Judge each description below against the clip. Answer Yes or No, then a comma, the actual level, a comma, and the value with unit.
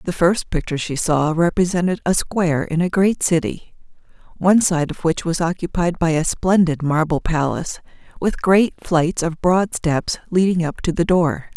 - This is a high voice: No, medium, 170 Hz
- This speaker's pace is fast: No, average, 175 wpm